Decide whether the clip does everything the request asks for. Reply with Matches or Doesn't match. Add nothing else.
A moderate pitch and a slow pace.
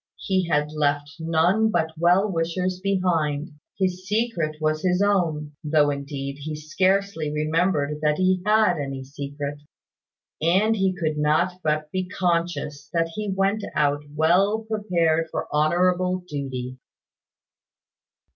Matches